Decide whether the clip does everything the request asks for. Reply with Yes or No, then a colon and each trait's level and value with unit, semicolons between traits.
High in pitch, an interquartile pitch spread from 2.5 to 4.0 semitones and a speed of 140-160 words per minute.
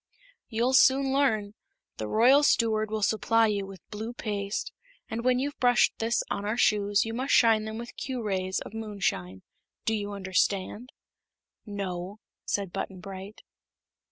Yes: high, 215 Hz; average, 2.8 semitones; average, 155 wpm